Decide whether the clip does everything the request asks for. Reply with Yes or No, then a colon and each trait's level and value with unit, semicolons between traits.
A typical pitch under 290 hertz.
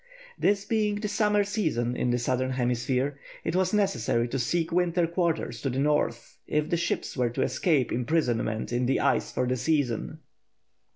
Yes: medium, 140 Hz